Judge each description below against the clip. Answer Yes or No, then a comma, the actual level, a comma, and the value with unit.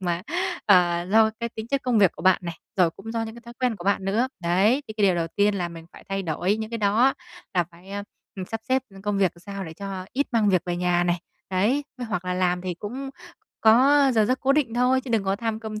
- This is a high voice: Yes, high, 205 Hz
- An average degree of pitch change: Yes, average, 4.3 semitones